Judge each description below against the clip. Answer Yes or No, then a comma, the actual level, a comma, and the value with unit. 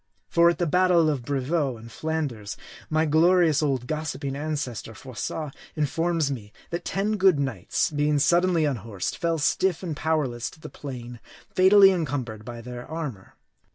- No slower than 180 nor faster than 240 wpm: No, average, 155 wpm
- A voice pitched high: No, medium, 150 Hz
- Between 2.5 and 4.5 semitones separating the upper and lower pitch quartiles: No, average, 4.9 semitones